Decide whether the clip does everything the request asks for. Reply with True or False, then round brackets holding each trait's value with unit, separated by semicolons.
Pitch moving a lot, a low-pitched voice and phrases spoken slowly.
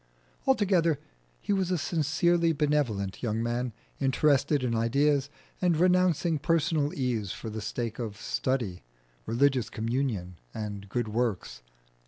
True (5.7 semitones; 130 Hz; 125 wpm)